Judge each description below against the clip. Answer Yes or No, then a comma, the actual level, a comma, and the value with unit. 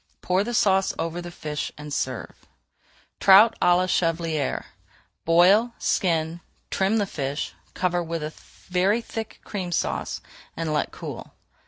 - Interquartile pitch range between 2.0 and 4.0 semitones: Yes, average, 3.1 semitones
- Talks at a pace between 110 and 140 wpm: Yes, slow, 135 wpm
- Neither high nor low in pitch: Yes, medium, 175 Hz